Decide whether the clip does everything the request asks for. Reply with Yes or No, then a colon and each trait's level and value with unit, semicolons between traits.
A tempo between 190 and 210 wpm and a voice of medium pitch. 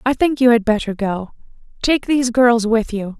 No: fast, 205 wpm; high, 235 Hz